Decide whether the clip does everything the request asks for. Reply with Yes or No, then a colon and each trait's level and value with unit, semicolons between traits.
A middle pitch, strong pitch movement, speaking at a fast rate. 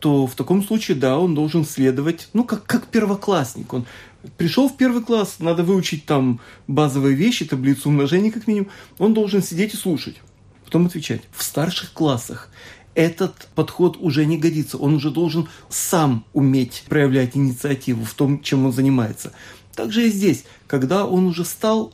Yes: medium, 155 Hz; wide, 5.7 semitones; fast, 165 wpm